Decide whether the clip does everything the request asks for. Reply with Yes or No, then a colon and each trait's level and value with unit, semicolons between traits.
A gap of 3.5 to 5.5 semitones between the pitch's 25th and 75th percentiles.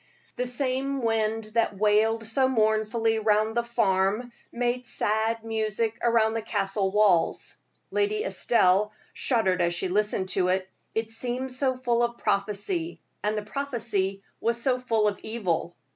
No: narrow, 2.5 semitones